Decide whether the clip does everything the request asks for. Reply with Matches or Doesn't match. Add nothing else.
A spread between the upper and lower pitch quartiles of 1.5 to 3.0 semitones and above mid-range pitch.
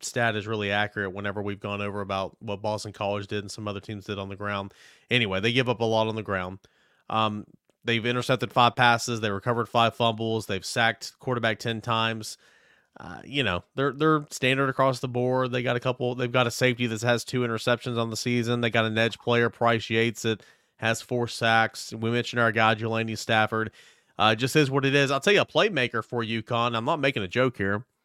Doesn't match